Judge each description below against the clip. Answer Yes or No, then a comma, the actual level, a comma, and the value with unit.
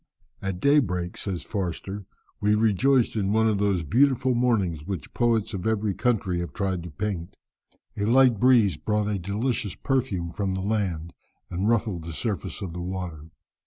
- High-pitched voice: No, low, 100 Hz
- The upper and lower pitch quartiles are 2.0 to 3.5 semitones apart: No, average, 4.0 semitones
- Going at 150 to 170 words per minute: Yes, average, 165 wpm